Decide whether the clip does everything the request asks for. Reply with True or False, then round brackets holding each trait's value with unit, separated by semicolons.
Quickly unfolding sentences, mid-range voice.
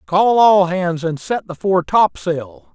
False (175 wpm; 165 Hz)